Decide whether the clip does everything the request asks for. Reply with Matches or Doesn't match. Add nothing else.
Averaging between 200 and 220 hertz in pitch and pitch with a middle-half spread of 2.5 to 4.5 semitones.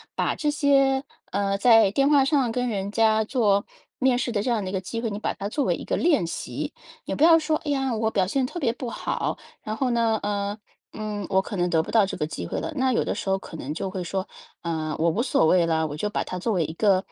Doesn't match